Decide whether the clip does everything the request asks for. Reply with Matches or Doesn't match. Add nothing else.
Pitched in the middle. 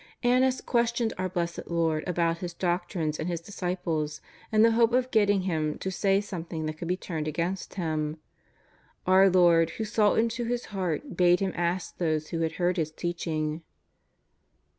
Matches